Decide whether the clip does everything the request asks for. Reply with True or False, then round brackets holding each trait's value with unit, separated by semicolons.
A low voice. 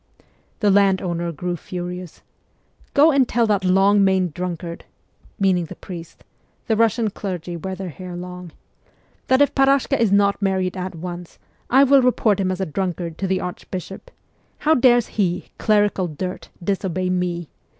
False (190 Hz)